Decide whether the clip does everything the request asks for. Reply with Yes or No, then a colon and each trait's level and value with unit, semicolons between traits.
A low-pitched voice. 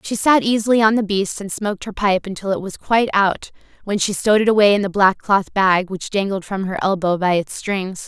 No: high, 200 Hz